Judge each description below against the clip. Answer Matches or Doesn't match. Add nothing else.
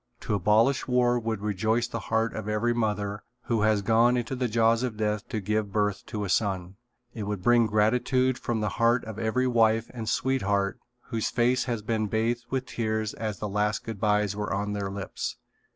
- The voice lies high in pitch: Doesn't match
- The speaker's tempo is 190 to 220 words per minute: Matches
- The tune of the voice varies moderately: Doesn't match